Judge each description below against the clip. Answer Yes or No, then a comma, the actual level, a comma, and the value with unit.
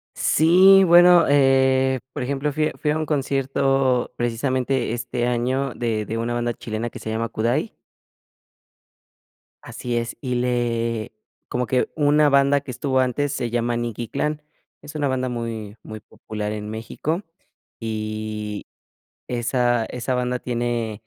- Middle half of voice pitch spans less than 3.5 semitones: Yes, average, 3.0 semitones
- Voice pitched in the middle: No, low, 125 Hz